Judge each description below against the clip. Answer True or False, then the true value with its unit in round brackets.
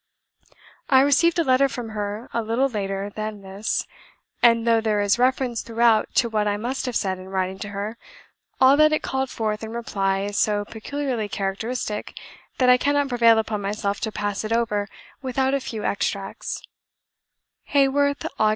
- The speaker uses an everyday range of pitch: True (3.9 semitones)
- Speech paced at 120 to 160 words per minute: False (175 wpm)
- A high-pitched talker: True (225 Hz)